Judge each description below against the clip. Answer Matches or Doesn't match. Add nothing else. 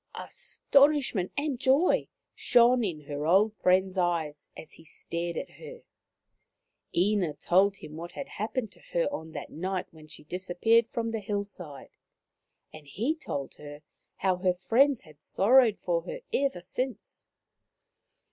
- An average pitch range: Doesn't match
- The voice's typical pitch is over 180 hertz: Matches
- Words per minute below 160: Matches